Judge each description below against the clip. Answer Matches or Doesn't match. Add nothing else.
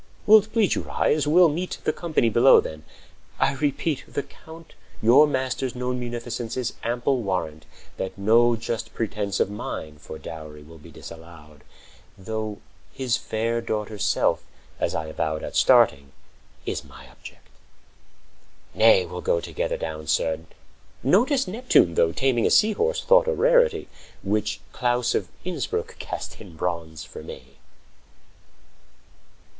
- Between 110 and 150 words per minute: Matches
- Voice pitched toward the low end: Matches